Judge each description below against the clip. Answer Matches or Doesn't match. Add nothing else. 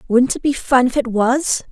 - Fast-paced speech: Matches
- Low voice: Doesn't match